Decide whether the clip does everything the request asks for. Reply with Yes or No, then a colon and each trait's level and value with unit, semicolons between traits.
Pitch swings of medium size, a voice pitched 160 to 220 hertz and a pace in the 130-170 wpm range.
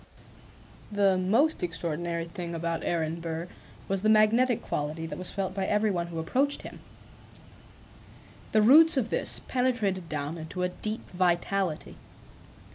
Yes: average, 4.3 semitones; medium, 185 Hz; average, 140 wpm